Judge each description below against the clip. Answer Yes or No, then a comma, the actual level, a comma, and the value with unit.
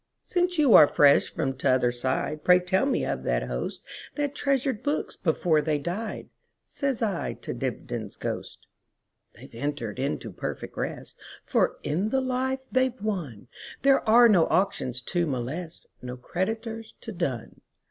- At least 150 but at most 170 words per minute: No, slow, 135 wpm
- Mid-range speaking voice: Yes, medium, 180 Hz